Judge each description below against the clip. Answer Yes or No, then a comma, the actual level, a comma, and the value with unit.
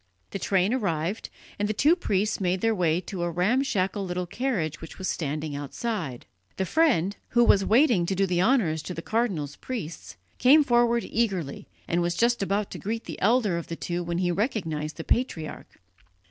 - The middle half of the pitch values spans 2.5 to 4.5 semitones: No, average, 5.3 semitones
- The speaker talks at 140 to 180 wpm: No, average, 190 wpm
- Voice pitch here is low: No, high, 190 Hz